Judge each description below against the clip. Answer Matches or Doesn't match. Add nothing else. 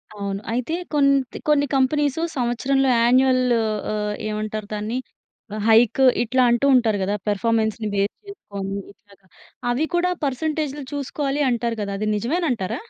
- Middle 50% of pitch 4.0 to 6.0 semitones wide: Matches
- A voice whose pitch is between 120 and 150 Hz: Doesn't match